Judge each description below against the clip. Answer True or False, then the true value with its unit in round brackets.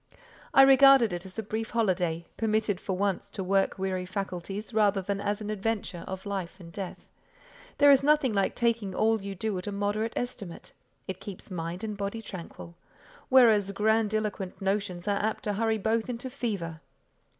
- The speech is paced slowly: False (175 wpm)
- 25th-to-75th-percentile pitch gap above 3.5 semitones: False (2.8 semitones)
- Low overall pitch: False (205 Hz)